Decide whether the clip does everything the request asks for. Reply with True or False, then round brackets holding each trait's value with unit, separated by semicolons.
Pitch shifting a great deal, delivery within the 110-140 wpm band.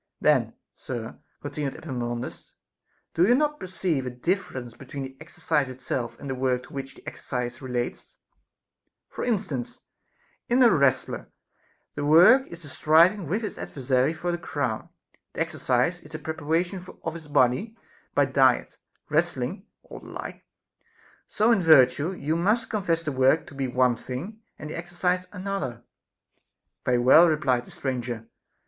False (5.7 semitones; 155 wpm)